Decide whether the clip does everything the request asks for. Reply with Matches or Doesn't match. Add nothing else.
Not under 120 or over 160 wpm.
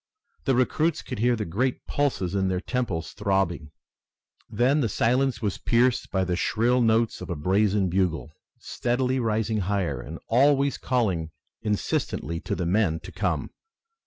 Matches